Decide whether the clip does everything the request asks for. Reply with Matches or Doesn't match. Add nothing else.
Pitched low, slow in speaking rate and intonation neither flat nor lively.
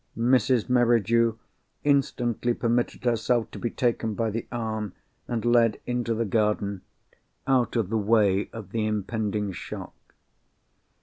Doesn't match